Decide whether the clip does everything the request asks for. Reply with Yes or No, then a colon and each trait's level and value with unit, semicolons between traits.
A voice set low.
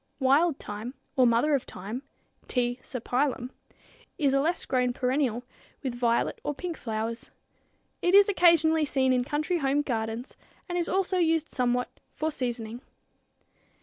No: very high, 265 Hz